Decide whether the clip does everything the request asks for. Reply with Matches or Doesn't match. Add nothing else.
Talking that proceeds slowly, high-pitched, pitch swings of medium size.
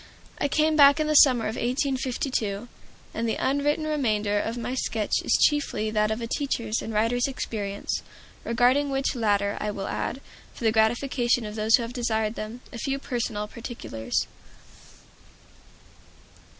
Doesn't match